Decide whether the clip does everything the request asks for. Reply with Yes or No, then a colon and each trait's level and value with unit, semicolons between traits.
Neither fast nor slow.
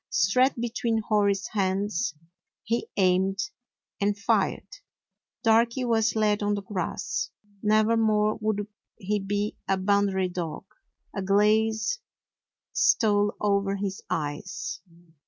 No: slow, 110 wpm